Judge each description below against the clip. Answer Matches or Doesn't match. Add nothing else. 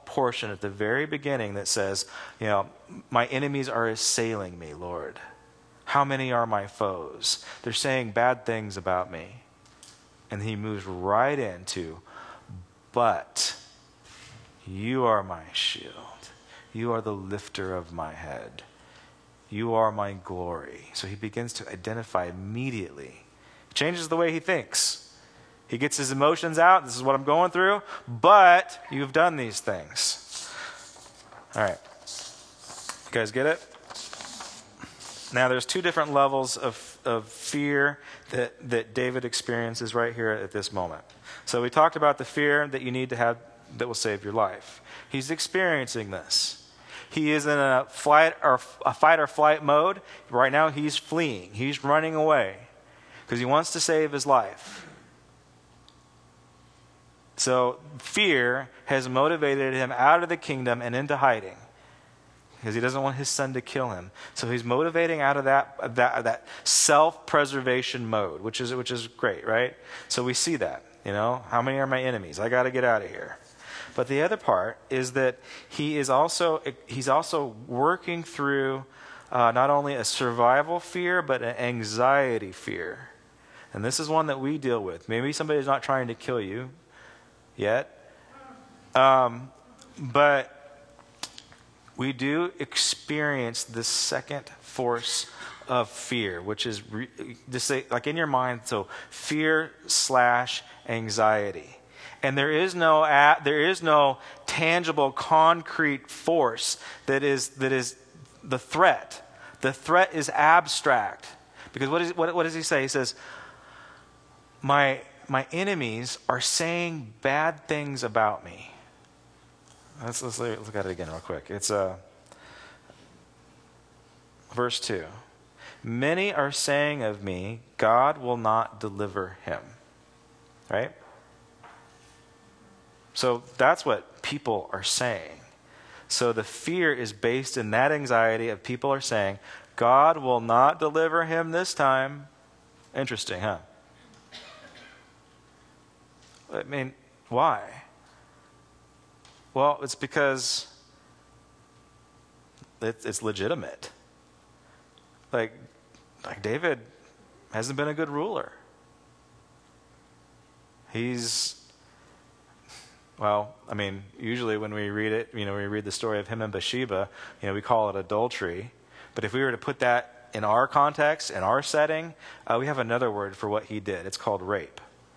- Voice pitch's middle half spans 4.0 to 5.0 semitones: Matches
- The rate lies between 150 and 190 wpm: Doesn't match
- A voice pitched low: Matches